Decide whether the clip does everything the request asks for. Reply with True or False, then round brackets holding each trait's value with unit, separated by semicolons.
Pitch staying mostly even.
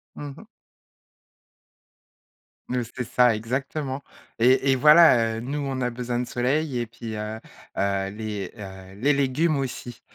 False (3.6 semitones)